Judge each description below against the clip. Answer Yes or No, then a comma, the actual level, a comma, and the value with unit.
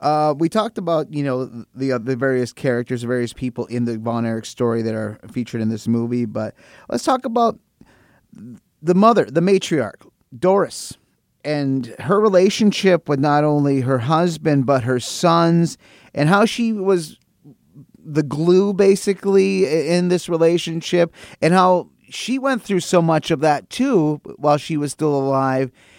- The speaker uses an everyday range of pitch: No, wide, 5.9 semitones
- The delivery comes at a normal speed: Yes, average, 160 wpm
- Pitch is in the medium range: Yes, medium, 150 Hz